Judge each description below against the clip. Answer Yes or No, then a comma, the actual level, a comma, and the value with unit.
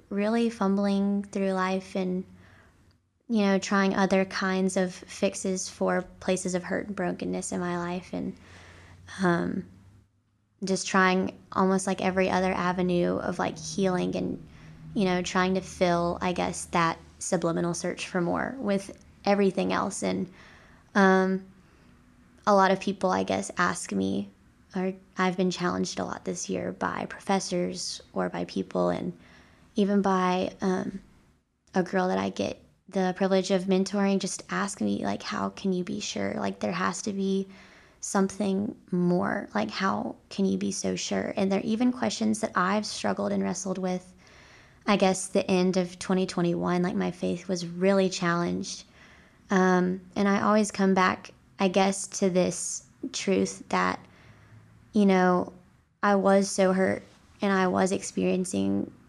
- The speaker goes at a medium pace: Yes, average, 155 wpm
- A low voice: No, medium, 185 Hz